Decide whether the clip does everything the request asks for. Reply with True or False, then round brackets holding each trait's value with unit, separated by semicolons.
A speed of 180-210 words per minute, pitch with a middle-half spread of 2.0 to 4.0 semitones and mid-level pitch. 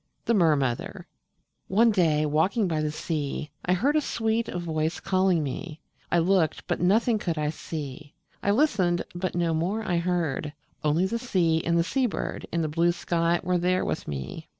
True (185 wpm; 3.4 semitones; 175 Hz)